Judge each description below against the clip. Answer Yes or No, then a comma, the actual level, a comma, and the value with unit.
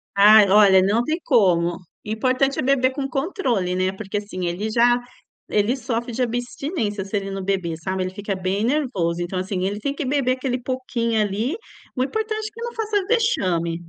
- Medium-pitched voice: No, high, 220 Hz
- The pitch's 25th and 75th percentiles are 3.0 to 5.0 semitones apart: No, wide, 5.6 semitones